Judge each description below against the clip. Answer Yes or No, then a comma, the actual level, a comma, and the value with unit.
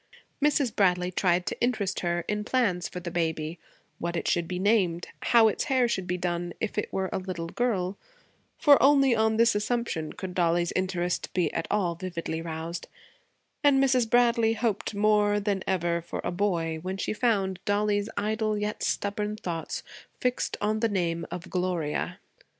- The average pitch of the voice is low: No, high, 195 Hz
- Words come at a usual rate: Yes, average, 175 wpm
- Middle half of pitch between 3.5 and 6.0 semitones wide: Yes, average, 4.0 semitones